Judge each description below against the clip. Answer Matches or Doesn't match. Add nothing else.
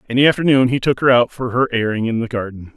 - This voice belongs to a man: Matches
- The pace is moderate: Doesn't match